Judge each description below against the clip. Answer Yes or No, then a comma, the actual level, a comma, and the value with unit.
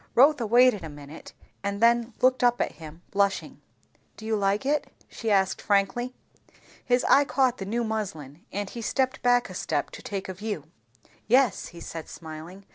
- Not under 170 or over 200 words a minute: Yes, average, 180 wpm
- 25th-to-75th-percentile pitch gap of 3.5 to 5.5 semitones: Yes, average, 4.6 semitones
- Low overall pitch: No, high, 210 Hz